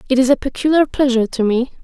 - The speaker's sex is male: No, female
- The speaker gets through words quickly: Yes, fast, 230 wpm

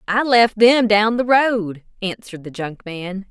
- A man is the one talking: No, female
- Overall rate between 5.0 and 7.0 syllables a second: No, 4.0 syllables/s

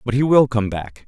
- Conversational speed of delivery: No, fast, 280 wpm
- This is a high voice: No, low, 115 Hz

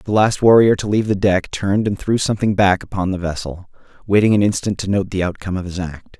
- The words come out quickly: Yes, fast, 240 wpm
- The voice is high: No, low, 100 Hz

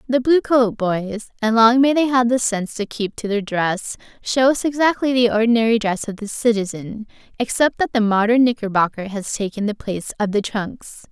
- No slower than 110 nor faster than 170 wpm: No, average, 195 wpm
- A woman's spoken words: Yes, female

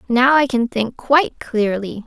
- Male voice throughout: No, female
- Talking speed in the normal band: Yes, average, 175 wpm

